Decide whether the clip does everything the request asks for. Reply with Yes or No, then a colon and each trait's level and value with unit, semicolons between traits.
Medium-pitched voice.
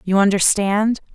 No: high, 200 Hz